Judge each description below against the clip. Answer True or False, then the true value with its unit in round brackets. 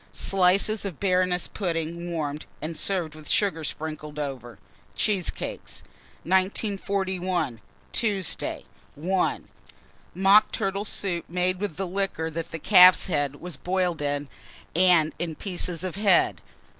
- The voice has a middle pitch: True (180 Hz)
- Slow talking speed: True (115 wpm)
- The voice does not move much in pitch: False (3.3 semitones)